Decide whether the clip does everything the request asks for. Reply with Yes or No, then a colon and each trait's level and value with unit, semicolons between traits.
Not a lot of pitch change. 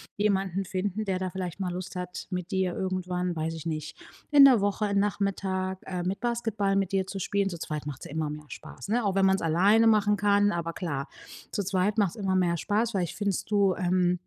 Yes: narrow, 2.3 semitones